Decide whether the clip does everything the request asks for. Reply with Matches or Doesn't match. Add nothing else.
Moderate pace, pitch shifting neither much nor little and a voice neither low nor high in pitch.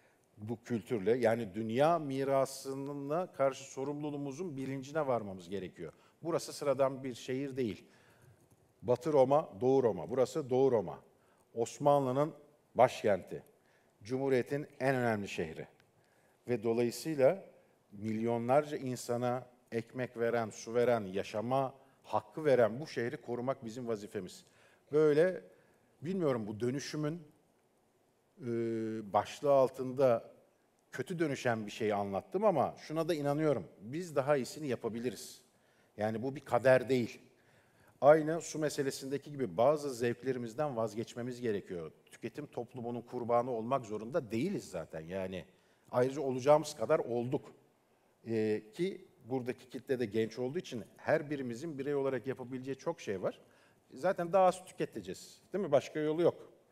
Doesn't match